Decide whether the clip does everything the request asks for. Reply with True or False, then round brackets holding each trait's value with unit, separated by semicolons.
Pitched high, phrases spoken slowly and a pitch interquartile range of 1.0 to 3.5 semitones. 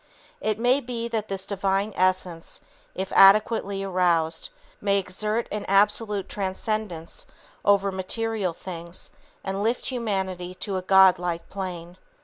True (195 Hz; 125 wpm; 2.4 semitones)